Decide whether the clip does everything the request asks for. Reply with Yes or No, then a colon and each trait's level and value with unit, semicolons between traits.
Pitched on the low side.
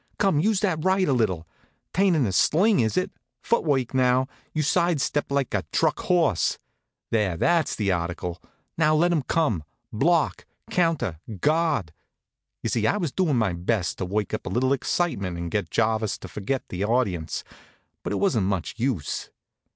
Yes: low, 130 Hz